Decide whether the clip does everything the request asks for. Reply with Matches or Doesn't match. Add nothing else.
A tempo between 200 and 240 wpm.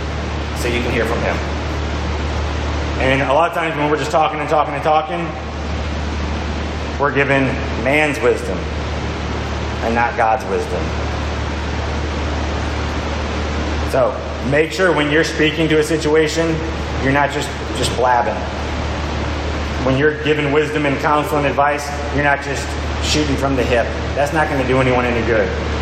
Doesn't match